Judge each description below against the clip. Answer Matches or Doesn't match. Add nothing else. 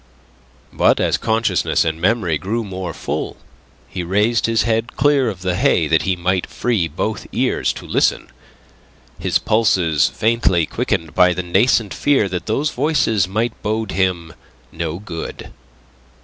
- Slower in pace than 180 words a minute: Matches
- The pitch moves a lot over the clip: Doesn't match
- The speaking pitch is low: Matches